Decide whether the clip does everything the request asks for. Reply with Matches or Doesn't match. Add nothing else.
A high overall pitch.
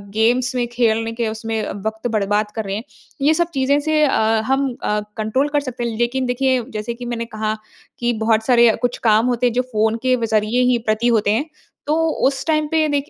Matches